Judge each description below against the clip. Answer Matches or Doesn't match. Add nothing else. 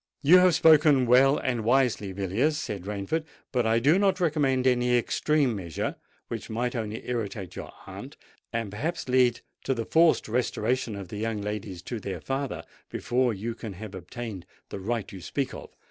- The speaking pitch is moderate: Doesn't match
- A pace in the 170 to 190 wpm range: Matches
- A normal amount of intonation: Matches